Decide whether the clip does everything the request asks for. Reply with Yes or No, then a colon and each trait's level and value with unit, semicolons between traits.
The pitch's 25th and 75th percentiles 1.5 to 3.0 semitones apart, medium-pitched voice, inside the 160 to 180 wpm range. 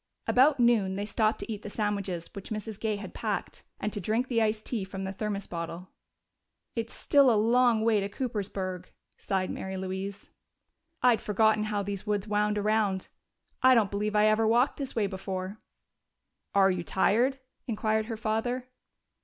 No: narrow, 2.4 semitones; high, 210 Hz; average, 170 wpm